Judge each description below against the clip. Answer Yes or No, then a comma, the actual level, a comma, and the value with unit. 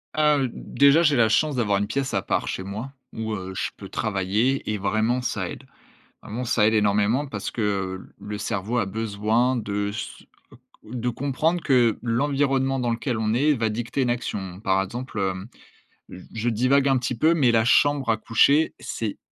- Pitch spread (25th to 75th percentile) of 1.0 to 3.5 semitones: No, average, 4.2 semitones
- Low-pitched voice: Yes, low, 115 Hz